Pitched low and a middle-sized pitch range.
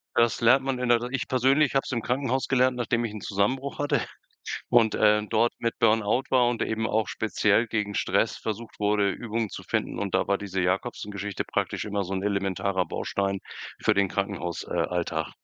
Yes: low, 110 Hz; average, 3.4 semitones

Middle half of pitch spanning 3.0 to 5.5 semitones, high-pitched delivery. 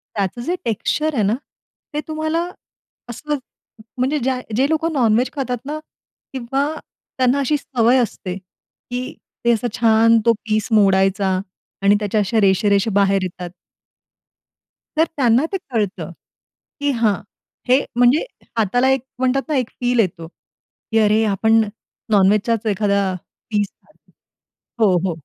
Yes: average, 4.3 semitones; high, 225 Hz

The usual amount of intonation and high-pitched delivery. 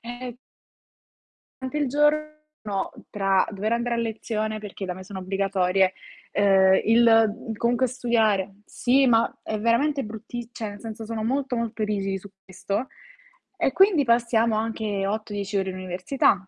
Yes: average, 3.3 semitones; high, 220 Hz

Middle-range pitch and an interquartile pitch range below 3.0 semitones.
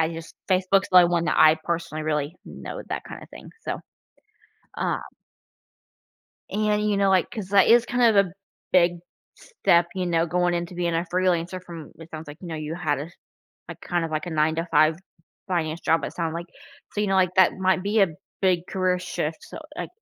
Yes: medium, 175 Hz; narrow, 2.4 semitones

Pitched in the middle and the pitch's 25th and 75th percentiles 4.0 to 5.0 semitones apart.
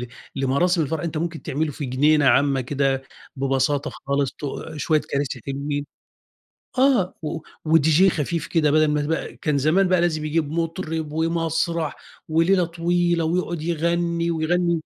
No: medium, 160 Hz; average, 2.8 semitones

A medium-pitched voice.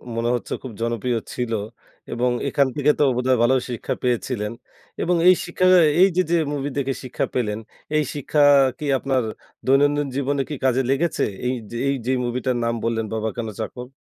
No: low, 130 Hz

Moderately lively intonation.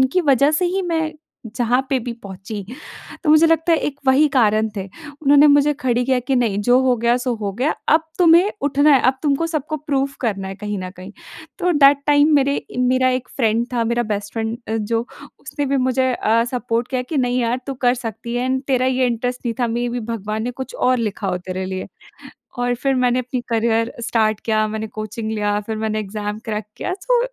Yes: average, 3.8 semitones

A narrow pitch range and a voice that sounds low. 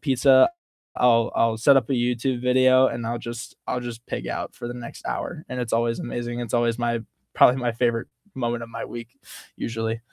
Yes: narrow, 1.3 semitones; low, 120 Hz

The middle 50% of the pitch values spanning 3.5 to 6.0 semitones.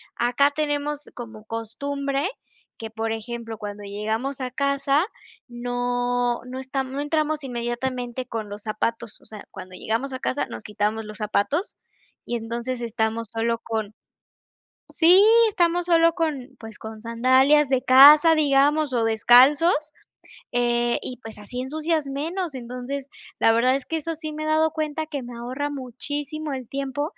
Yes: average, 4.1 semitones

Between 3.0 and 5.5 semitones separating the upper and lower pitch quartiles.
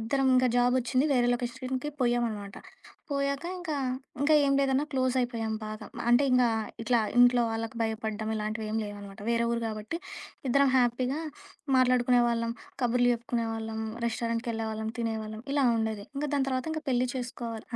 No: narrow, 2.4 semitones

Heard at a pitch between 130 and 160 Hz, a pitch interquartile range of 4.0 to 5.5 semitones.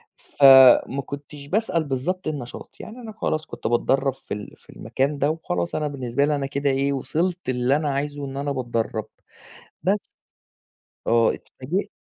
No: medium, 140 Hz; average, 2.9 semitones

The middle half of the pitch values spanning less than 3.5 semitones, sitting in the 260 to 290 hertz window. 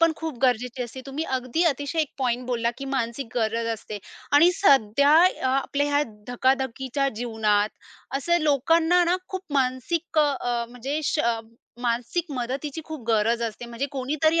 No: average, 4.0 semitones; very high, 265 Hz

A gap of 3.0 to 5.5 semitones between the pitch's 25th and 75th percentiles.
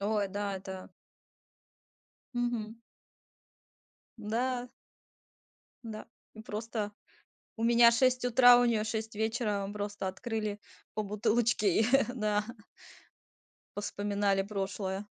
No: narrow, 2.4 semitones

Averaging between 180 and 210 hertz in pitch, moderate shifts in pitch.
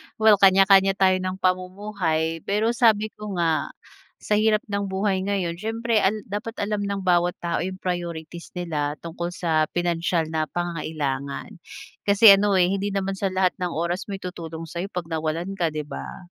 Yes: medium, 185 Hz; average, 3.2 semitones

